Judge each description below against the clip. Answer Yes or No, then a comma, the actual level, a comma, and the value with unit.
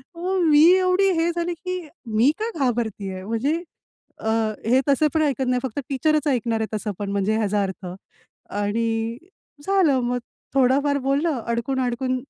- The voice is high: Yes, very high, 255 Hz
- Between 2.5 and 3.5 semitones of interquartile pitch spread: No, wide, 5.4 semitones